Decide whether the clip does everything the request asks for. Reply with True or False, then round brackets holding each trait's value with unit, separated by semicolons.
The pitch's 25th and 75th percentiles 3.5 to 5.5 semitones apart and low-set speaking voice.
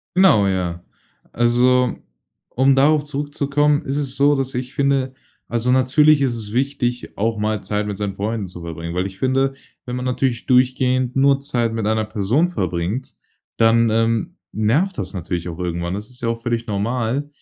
True (4.3 semitones; 120 Hz)